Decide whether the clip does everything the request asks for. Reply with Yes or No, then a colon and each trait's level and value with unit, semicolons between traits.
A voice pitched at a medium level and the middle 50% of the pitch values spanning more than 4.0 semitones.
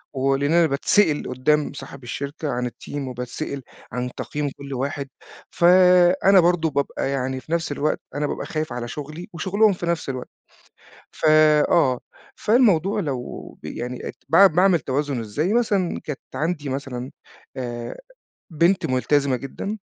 Yes: medium, 145 Hz; average, 4.7 semitones